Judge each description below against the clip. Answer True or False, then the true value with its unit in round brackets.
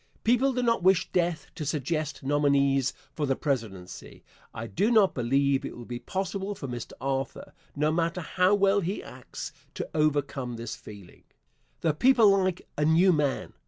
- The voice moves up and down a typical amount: False (5.8 semitones)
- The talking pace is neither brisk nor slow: True (165 wpm)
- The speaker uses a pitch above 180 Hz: False (155 Hz)